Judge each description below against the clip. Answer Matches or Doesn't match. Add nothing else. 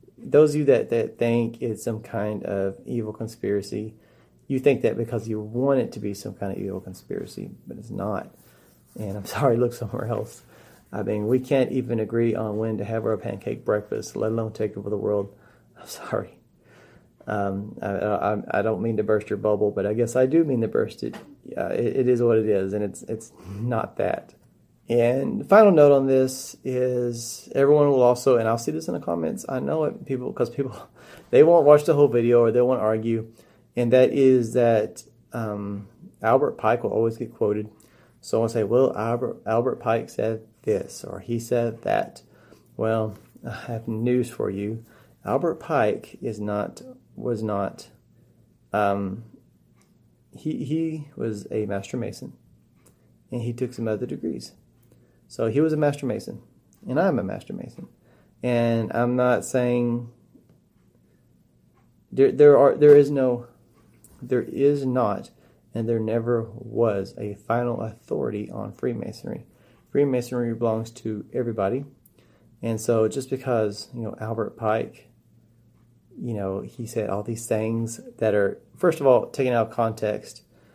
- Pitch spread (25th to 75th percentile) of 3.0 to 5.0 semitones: Doesn't match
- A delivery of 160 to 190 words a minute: Matches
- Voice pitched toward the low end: Matches